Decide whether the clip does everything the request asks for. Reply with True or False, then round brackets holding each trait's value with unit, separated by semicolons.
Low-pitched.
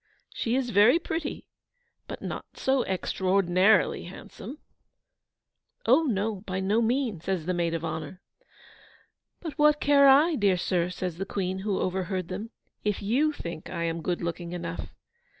False (190 Hz)